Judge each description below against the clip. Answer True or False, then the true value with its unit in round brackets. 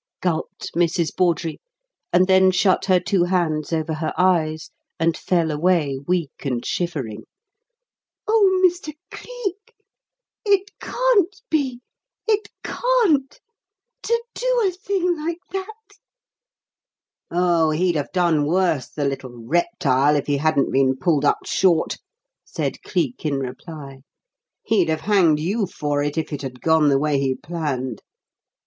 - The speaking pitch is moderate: True (170 Hz)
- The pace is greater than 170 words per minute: False (135 wpm)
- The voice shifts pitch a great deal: True (7.3 semitones)